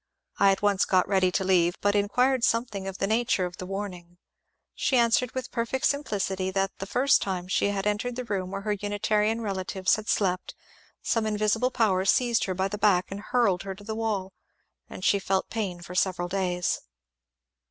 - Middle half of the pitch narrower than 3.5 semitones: Yes, average, 2.7 semitones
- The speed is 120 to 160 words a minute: No, average, 195 wpm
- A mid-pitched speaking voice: No, high, 200 Hz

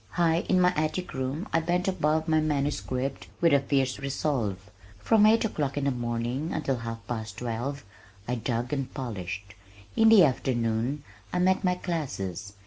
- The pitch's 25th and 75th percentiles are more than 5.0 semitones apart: Yes, wide, 5.5 semitones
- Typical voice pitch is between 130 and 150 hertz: Yes, medium, 140 Hz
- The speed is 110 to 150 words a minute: No, average, 165 wpm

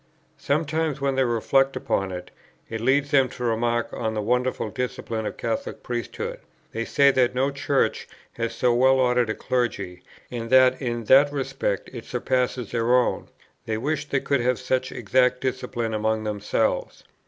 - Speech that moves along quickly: No, average, 170 wpm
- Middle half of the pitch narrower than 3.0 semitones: Yes, narrow, 2.6 semitones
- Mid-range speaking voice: No, low, 125 Hz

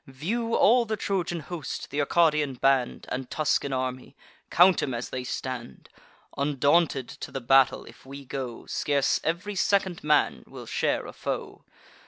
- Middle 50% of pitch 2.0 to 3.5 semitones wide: No, average, 4.8 semitones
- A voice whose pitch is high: No, medium, 145 Hz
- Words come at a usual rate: Yes, average, 155 wpm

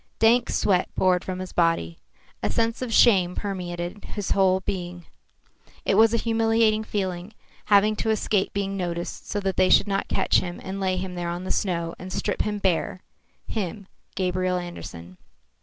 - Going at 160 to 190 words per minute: Yes, average, 175 wpm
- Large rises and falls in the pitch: No, average, 2.8 semitones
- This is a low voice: No, high, 190 Hz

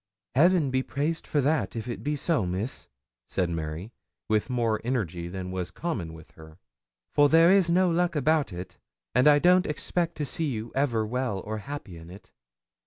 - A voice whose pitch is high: No, low, 125 Hz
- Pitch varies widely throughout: Yes, wide, 8.5 semitones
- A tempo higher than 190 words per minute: No, average, 185 wpm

